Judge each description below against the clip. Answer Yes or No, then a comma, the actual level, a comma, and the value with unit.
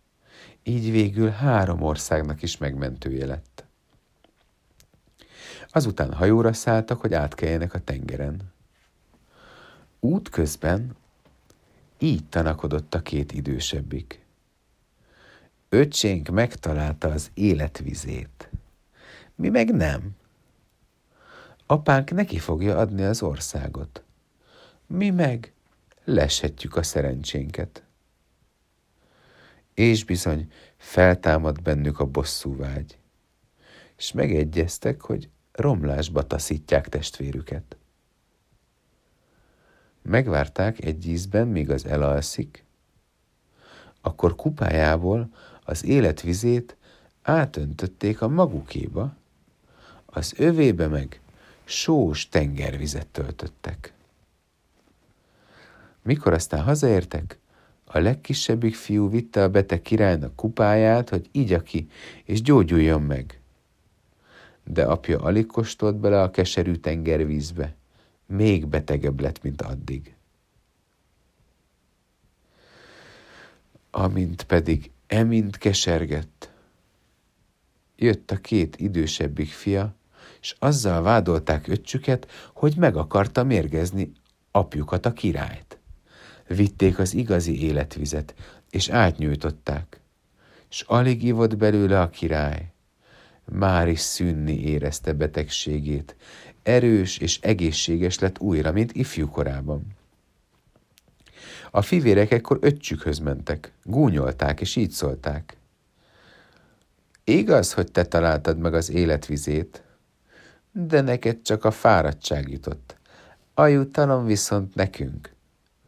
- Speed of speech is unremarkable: No, slow, 90 wpm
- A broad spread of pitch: Yes, wide, 6.3 semitones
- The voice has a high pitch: No, very low, 85 Hz